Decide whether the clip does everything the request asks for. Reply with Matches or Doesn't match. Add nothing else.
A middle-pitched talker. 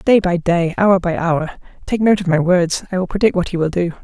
Matches